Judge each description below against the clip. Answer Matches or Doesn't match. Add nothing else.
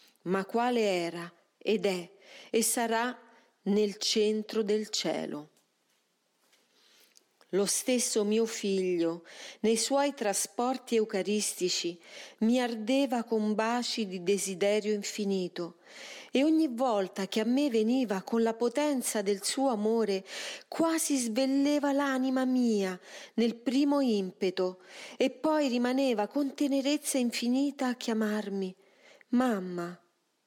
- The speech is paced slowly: Matches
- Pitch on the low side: Doesn't match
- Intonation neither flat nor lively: Matches